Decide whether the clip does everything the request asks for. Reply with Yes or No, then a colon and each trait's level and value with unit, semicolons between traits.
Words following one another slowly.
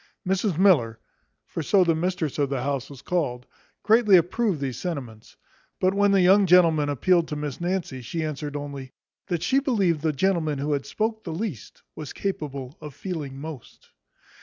No: average, 175 wpm